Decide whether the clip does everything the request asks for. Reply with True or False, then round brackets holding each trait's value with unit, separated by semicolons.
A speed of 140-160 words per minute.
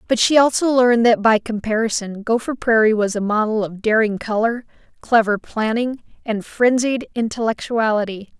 True (145 wpm)